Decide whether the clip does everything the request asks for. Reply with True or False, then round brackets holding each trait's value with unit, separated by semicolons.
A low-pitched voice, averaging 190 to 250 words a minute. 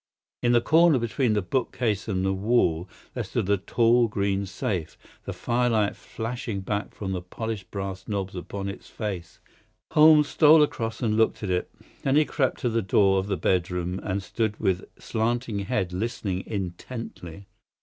False (105 Hz; 170 wpm)